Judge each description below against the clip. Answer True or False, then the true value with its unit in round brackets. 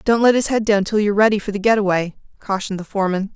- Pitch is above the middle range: True (205 Hz)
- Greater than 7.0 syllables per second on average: True (7.3 syllables/s)